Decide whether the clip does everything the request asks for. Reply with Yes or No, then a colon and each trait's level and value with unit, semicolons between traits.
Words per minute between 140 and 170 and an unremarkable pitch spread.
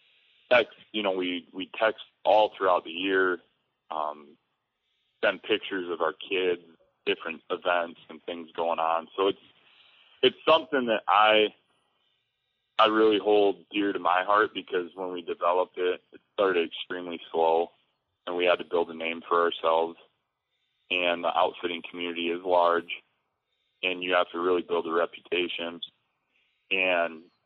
Yes: average, 150 wpm; average, 3.4 semitones